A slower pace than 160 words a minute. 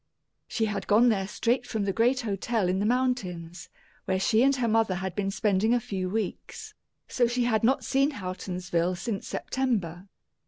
No: average, 180 wpm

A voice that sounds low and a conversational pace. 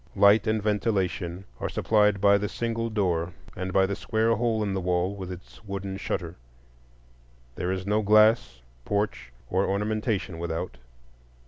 Yes: low, 100 Hz; average, 150 wpm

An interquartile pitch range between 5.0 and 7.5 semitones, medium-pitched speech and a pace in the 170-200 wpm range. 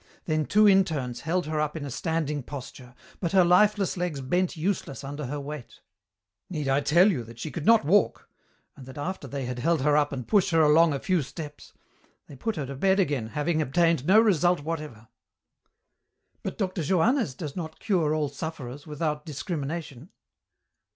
No: average, 3.9 semitones; medium, 155 Hz; average, 185 wpm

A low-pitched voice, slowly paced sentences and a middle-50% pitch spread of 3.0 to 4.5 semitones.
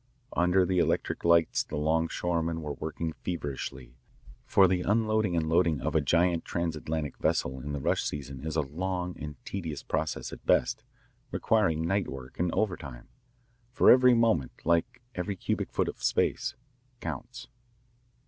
No: very low, 85 Hz; average, 150 wpm; average, 3.5 semitones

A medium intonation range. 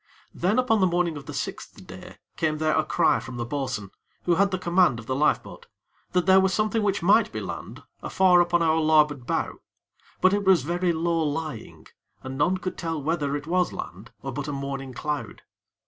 Yes: average, 4.4 semitones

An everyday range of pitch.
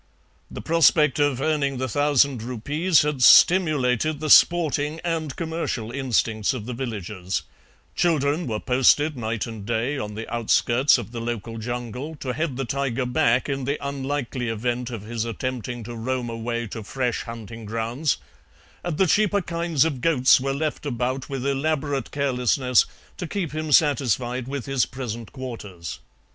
Yes: average, 3.9 semitones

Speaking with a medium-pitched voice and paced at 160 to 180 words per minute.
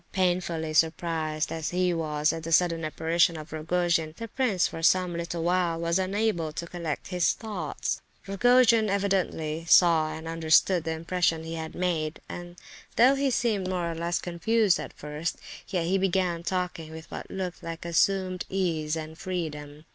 Yes: medium, 170 Hz; average, 165 wpm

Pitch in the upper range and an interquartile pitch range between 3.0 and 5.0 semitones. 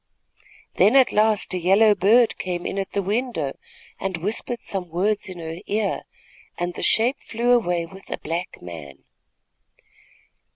Yes: high, 195 Hz; average, 4.0 semitones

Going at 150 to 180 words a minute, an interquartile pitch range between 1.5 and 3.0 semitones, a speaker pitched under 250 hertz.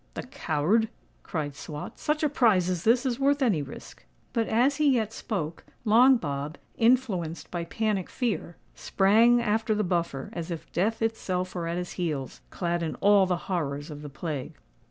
No: average, 175 wpm; wide, 5.5 semitones; medium, 185 Hz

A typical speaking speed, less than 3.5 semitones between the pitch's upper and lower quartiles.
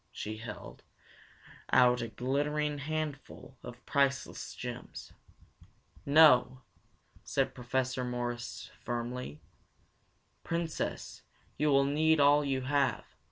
No: slow, 95 wpm; average, 3.1 semitones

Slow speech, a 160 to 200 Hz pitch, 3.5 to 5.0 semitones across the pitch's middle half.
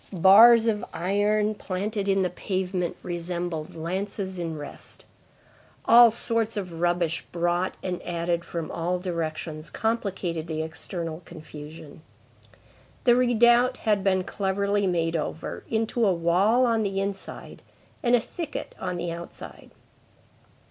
Yes: slow, 125 wpm; medium, 185 Hz; average, 3.8 semitones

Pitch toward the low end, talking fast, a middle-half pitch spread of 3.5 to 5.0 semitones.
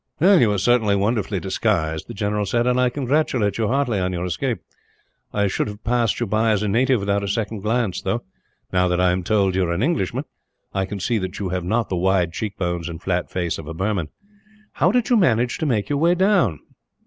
Yes: low, 105 Hz; fast, 230 wpm; average, 4.5 semitones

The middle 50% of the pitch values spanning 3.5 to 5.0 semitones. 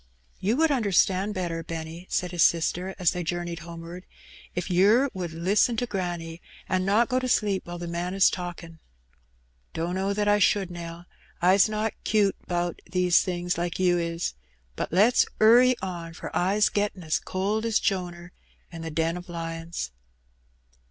No: average, 2.9 semitones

